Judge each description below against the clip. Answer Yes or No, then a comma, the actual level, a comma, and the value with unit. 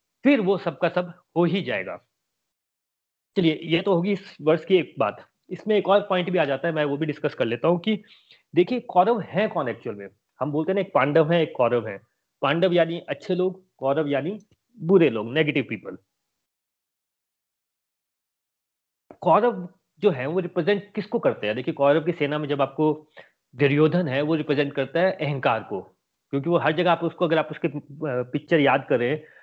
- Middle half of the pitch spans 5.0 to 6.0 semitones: No, average, 4.2 semitones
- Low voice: No, medium, 165 Hz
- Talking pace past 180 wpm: Yes, fast, 190 wpm